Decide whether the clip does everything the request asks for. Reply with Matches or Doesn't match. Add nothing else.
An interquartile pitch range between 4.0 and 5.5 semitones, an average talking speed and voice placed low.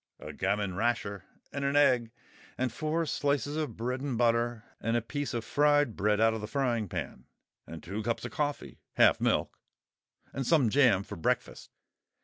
Matches